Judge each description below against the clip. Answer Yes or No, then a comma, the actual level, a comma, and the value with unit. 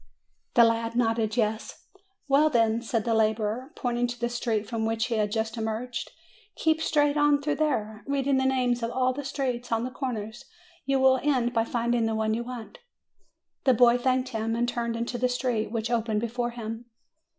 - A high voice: Yes, high, 240 Hz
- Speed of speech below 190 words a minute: No, average, 195 wpm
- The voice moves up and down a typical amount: No, narrow, 2.2 semitones